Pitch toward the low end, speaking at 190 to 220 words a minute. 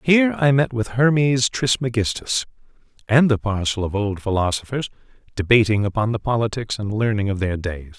No: low, 115 Hz; average, 160 wpm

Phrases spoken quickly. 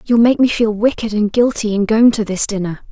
Yes: fast, 245 wpm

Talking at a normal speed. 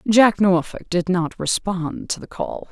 Yes: average, 175 wpm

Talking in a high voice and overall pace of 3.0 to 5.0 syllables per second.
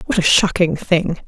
No: medium, 180 Hz; 4.7 syllables/s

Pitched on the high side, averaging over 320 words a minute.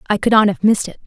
Yes: high, 200 Hz; fast, 335 wpm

